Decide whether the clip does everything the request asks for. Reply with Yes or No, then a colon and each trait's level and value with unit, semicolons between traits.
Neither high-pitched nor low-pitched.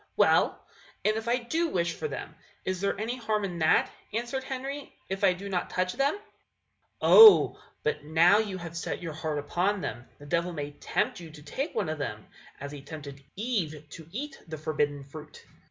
Yes: medium, 180 Hz